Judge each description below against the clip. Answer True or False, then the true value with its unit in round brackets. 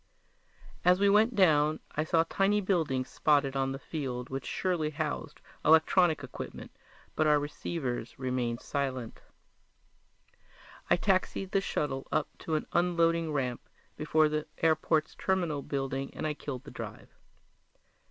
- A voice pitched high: False (155 Hz)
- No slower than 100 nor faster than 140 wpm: True (135 wpm)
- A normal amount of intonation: True (3.9 semitones)